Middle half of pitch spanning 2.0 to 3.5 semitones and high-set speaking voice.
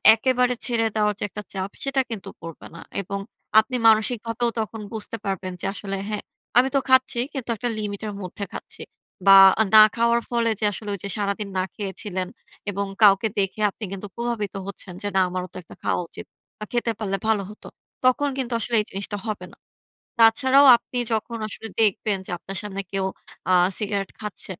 Yes: average, 3.0 semitones; high, 210 Hz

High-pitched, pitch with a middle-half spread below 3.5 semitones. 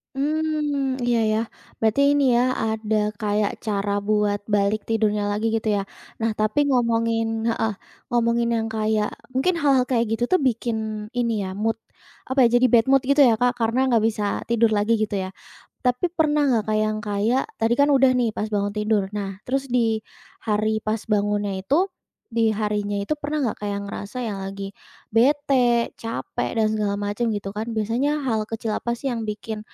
Yes: high, 225 Hz; average, 2.8 semitones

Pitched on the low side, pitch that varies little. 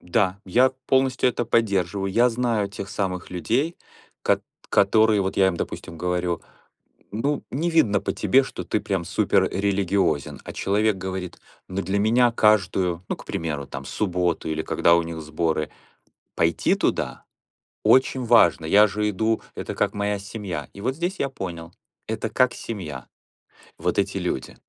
No: low, 100 Hz; average, 4.2 semitones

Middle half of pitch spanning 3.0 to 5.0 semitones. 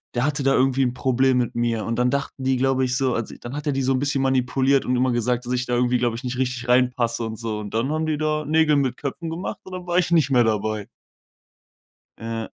No: narrow, 2.5 semitones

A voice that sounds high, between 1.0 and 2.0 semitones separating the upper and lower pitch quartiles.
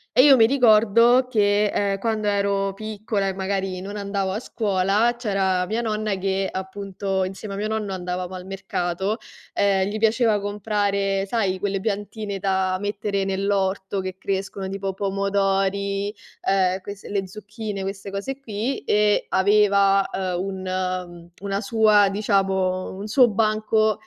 Yes: high, 200 Hz; narrow, 1.7 semitones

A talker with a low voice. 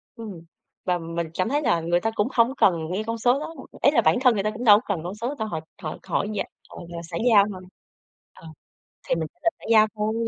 No: high, 210 Hz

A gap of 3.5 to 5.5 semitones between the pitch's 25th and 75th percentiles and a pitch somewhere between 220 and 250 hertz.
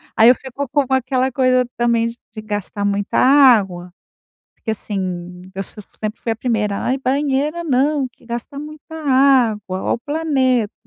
Yes: average, 4.4 semitones; high, 245 Hz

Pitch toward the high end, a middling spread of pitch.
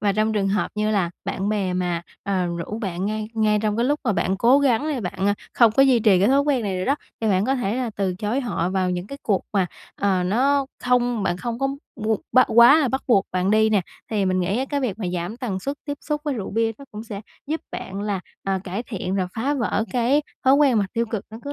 Yes: high, 215 Hz; average, 4.5 semitones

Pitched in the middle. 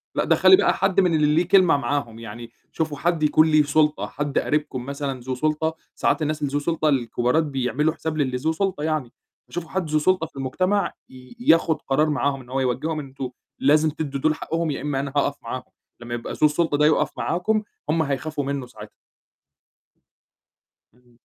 Yes: medium, 150 Hz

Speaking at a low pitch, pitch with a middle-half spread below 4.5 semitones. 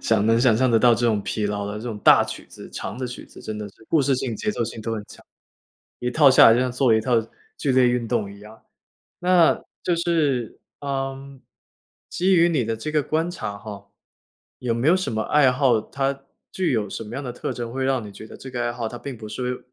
Yes: low, 125 Hz; average, 3.7 semitones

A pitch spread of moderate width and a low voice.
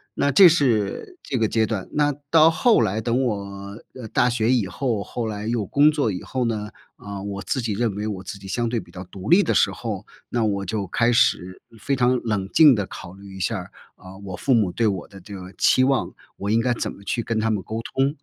Yes: average, 3.9 semitones; low, 110 Hz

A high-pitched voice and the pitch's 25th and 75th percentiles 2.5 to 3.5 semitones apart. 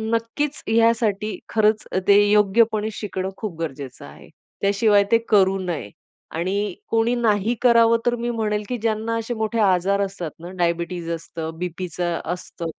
No: high, 205 Hz; average, 4.2 semitones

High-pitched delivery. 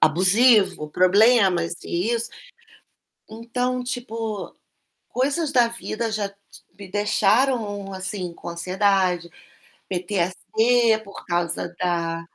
Yes: high, 200 Hz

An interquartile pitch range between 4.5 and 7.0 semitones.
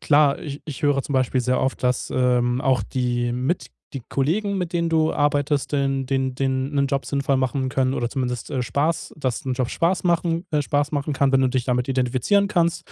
No: narrow, 2.6 semitones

